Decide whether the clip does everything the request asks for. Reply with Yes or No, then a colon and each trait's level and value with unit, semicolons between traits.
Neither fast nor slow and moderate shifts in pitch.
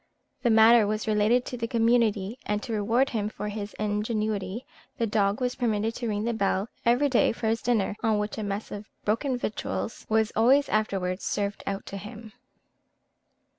No: average, 180 wpm; narrow, 2.1 semitones